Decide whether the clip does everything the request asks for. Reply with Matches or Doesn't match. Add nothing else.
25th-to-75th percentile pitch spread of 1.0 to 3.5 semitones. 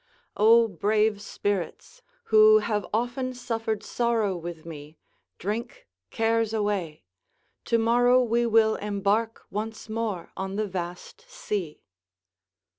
Matches